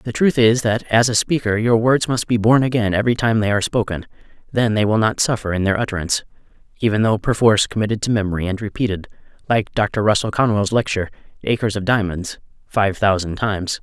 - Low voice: Yes, low, 110 Hz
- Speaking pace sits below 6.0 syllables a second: No, 6.1 syllables/s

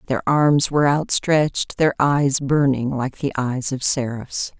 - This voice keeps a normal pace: Yes, average, 155 wpm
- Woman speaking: Yes, female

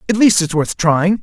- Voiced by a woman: No, male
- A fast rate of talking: Yes, fast, 245 wpm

